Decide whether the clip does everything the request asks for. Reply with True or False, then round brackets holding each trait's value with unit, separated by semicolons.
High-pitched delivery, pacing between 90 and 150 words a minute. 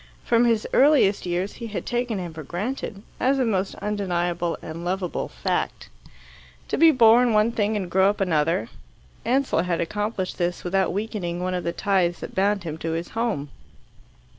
False (195 Hz; 175 wpm)